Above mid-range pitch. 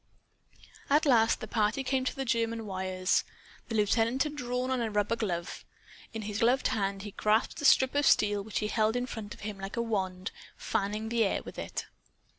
Yes: high, 220 Hz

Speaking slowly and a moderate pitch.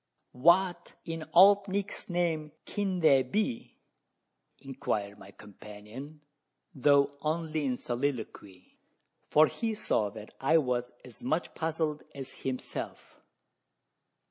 Yes: slow, 110 wpm; medium, 145 Hz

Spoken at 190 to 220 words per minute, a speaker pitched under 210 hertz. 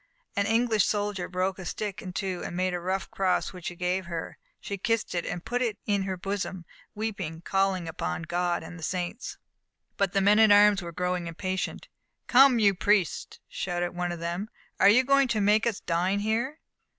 Yes: average, 200 wpm; high, 190 Hz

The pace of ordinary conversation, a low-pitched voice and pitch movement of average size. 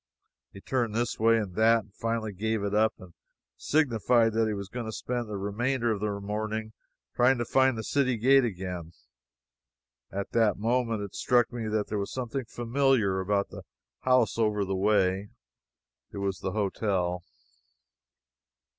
Yes: average, 165 wpm; low, 110 Hz; average, 3.0 semitones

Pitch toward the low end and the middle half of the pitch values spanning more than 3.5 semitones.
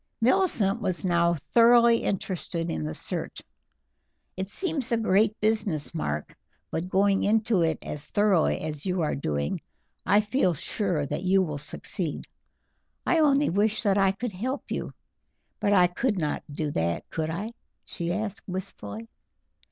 No: high, 190 Hz; average, 5.1 semitones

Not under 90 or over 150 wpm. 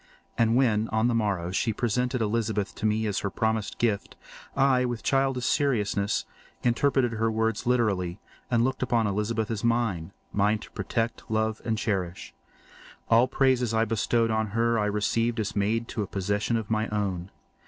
No: average, 165 wpm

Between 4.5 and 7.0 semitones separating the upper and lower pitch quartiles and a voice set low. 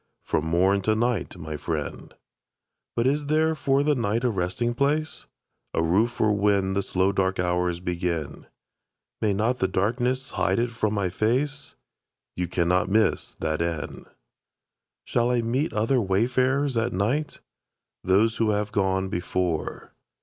Yes: average, 4.8 semitones; low, 105 Hz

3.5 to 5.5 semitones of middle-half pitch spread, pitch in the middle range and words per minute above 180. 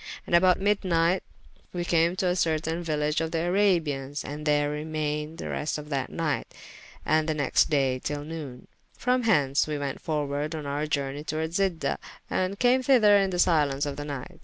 No: average, 3.1 semitones; medium, 155 Hz; average, 190 wpm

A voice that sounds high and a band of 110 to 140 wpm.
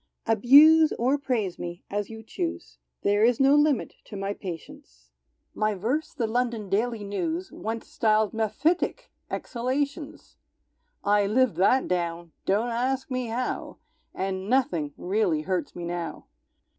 Yes: high, 215 Hz; slow, 135 wpm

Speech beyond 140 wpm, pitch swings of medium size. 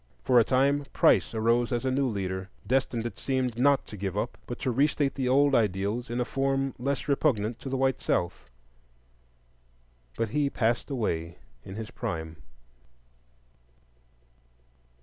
Yes: average, 155 wpm; average, 3.8 semitones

